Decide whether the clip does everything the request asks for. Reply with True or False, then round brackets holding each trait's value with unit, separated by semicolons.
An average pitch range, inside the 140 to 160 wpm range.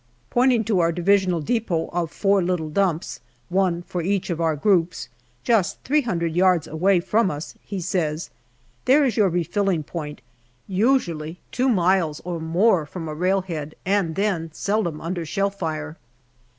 True (3.5 semitones; 155 wpm)